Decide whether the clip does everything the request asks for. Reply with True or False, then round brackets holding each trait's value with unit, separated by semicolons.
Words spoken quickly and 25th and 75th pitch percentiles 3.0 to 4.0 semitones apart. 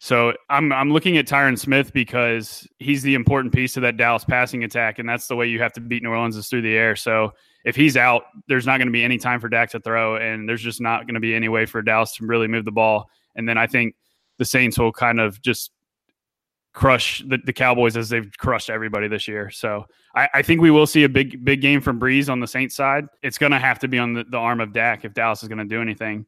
False (270 wpm; 2.6 semitones)